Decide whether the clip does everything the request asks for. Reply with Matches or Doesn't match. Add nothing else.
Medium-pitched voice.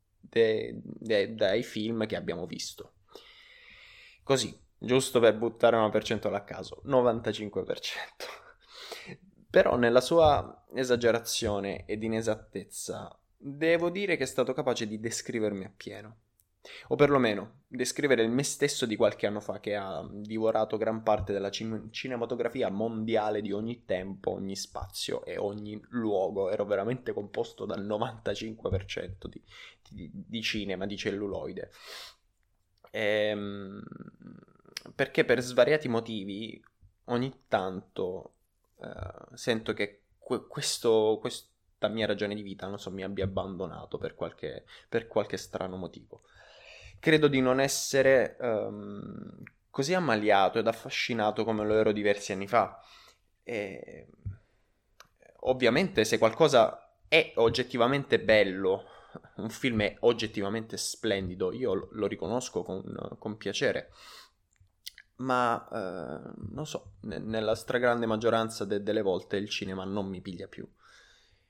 Doesn't match